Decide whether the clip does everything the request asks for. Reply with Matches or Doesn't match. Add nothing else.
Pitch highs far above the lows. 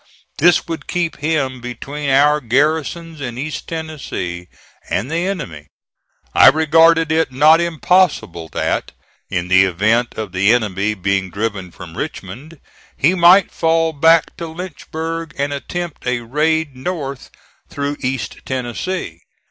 Matches